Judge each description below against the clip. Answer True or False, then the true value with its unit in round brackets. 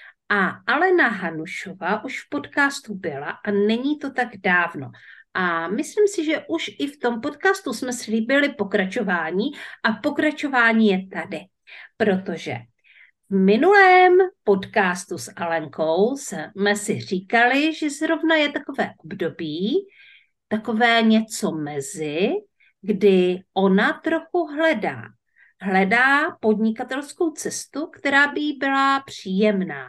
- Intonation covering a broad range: True (7.4 semitones)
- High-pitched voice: True (225 Hz)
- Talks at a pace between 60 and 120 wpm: True (115 wpm)